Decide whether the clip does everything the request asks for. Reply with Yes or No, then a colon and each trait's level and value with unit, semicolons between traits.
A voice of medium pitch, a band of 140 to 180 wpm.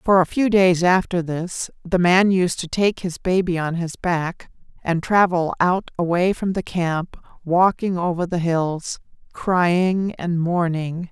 Yes: medium, 175 Hz; average, 160 wpm